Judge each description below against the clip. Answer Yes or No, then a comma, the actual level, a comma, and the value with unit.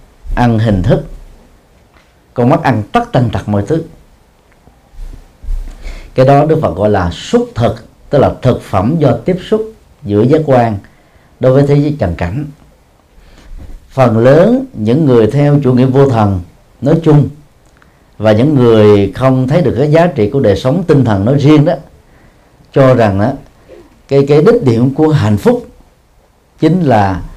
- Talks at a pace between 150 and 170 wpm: Yes, slow, 165 wpm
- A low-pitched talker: Yes, low, 130 Hz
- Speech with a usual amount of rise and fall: No, wide, 6.0 semitones